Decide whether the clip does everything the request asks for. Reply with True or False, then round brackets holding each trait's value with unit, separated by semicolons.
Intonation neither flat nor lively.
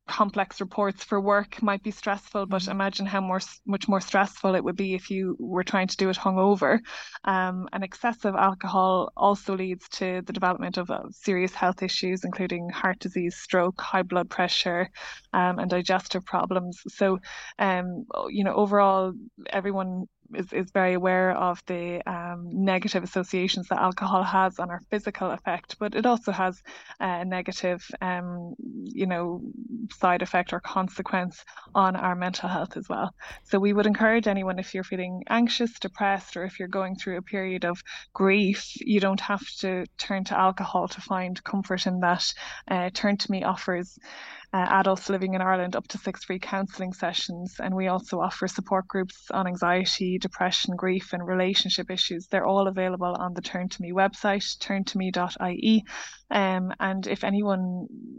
False (1.4 semitones)